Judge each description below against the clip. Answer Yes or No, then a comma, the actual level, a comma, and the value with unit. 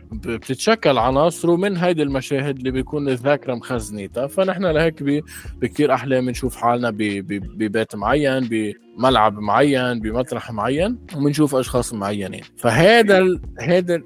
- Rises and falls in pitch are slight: No, average, 4.6 semitones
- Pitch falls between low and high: No, low, 130 Hz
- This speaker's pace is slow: No, average, 110 wpm